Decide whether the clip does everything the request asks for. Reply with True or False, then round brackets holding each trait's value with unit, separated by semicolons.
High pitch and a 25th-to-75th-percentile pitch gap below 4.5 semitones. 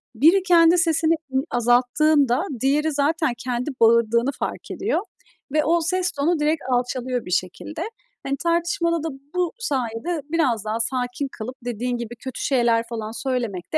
False (270 Hz; 5.3 semitones)